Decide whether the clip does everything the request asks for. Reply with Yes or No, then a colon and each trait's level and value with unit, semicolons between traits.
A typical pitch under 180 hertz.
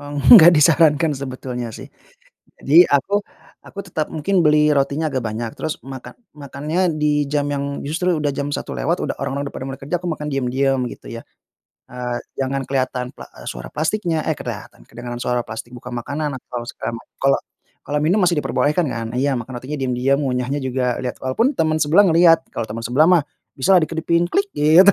Yes: medium, 140 Hz